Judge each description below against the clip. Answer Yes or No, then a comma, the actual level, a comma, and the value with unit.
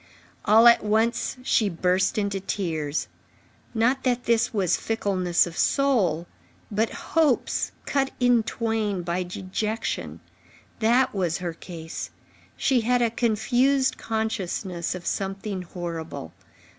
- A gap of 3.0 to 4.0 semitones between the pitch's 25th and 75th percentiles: No, average, 4.6 semitones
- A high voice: Yes, high, 210 Hz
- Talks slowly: Yes, slow, 115 wpm